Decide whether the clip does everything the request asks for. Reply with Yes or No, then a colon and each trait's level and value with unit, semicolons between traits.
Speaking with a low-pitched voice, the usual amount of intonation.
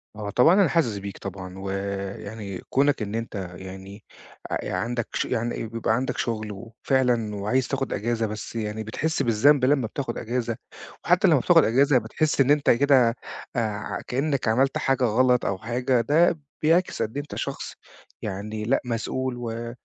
Yes: low, 115 Hz; average, 3.8 semitones